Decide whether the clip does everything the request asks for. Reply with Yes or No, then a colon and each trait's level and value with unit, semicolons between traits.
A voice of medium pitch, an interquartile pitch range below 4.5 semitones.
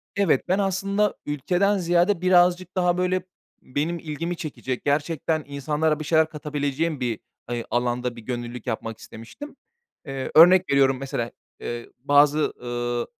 No: medium, 150 Hz; wide, 5.6 semitones